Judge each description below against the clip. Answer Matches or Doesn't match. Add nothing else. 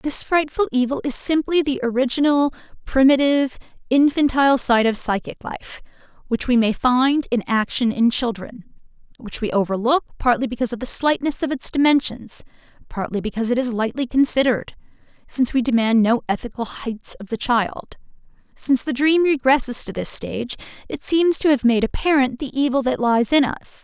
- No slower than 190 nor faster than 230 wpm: Doesn't match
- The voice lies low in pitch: Doesn't match